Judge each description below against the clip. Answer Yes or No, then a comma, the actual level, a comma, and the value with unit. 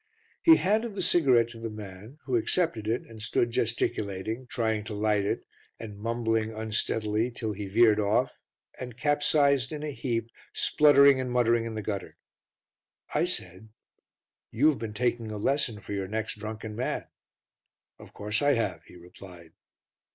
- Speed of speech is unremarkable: Yes, average, 160 wpm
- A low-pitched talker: Yes, low, 115 Hz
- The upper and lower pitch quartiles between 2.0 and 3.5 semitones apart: Yes, average, 3.2 semitones